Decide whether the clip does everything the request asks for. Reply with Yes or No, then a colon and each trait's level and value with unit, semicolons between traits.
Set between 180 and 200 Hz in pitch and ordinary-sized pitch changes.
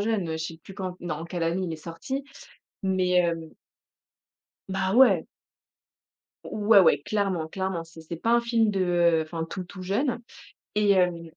Yes: medium, 185 Hz; average, 3.5 semitones